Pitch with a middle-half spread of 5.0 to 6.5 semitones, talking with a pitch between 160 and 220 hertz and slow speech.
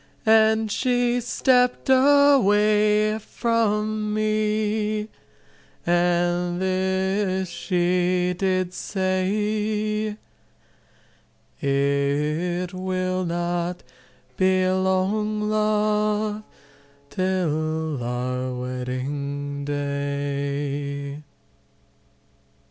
Yes: wide, 5.6 semitones; medium, 185 Hz; slow, 55 wpm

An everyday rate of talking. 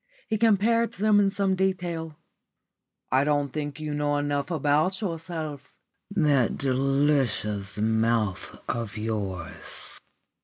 No: slow, 120 wpm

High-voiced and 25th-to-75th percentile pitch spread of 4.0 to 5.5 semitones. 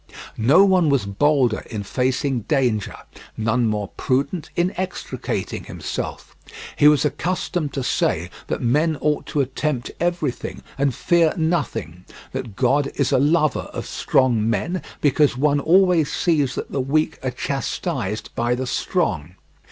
No: medium, 140 Hz; average, 4.3 semitones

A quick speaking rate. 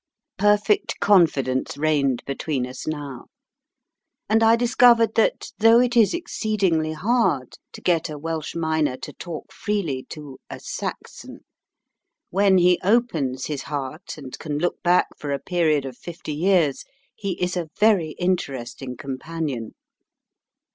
No: slow, 135 wpm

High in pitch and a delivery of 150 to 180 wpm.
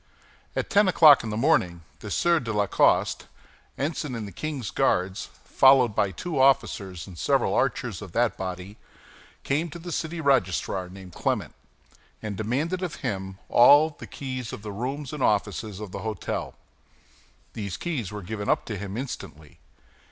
No: low, 110 Hz; average, 165 wpm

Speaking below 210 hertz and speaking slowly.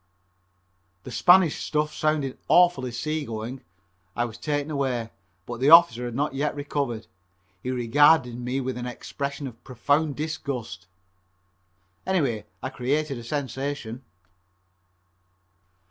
Yes: low, 135 Hz; slow, 120 wpm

